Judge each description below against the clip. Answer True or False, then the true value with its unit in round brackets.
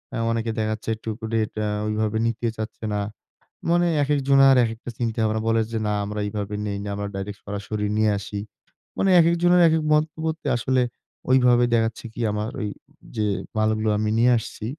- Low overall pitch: True (110 Hz)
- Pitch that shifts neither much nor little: True (3.4 semitones)